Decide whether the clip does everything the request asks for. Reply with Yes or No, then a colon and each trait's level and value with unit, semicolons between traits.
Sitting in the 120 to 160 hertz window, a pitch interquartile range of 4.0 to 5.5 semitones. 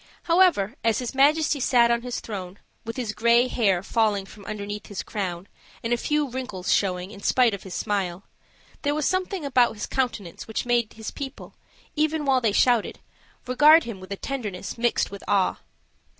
No: high, 230 Hz; average, 4.7 semitones